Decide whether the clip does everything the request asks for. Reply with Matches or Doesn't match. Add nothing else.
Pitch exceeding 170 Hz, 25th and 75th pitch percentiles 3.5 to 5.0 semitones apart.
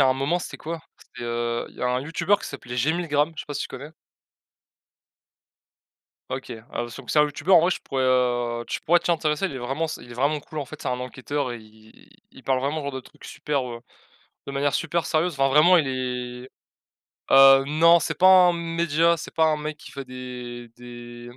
Doesn't match